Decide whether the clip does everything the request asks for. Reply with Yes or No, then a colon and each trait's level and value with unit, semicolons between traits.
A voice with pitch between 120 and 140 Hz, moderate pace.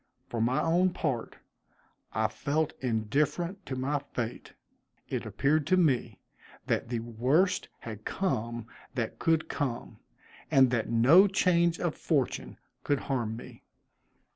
No: low, 135 Hz; slow, 130 wpm